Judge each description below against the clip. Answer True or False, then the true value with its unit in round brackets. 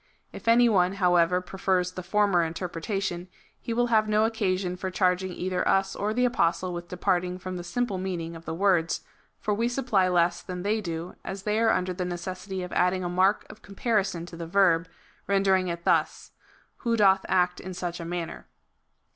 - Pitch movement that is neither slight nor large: False (2.3 semitones)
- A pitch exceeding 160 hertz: True (185 Hz)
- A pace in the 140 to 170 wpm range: False (200 wpm)